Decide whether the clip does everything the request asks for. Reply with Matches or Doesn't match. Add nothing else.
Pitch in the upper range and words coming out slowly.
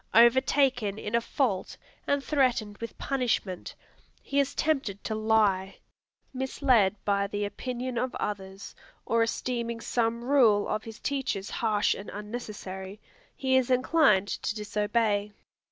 Matches